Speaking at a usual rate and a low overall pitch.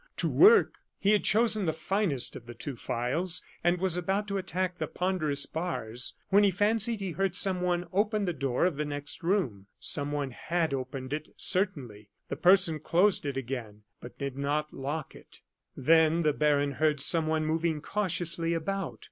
No: average, 175 wpm; medium, 160 Hz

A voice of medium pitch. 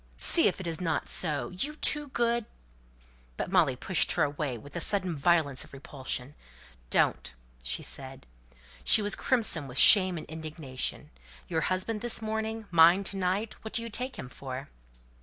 Yes: medium, 175 Hz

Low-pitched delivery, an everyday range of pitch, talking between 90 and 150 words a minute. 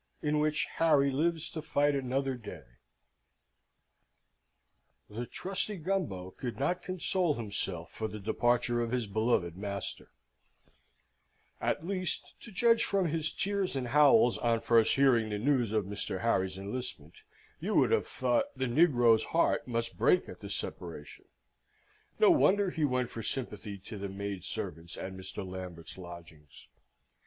No: low, 120 Hz; wide, 7.6 semitones; average, 145 wpm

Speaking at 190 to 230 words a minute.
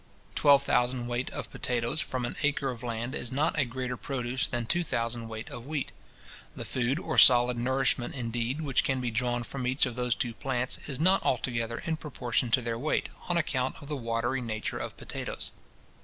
Yes: average, 200 wpm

